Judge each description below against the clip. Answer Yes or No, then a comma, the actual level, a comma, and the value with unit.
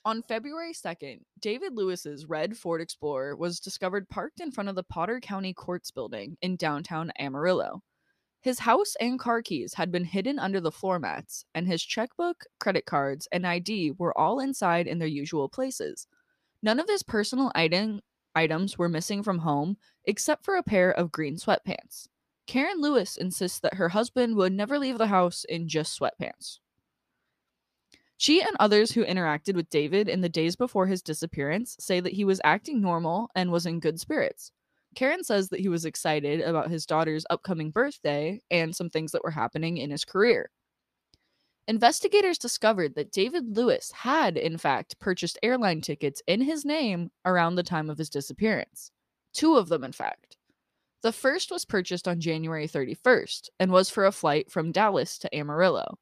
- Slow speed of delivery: No, average, 175 wpm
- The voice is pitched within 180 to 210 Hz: Yes, medium, 185 Hz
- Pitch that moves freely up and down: Yes, wide, 6.0 semitones